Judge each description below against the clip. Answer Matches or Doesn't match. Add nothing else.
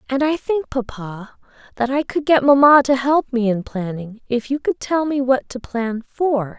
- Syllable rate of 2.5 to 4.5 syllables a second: Matches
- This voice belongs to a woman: Matches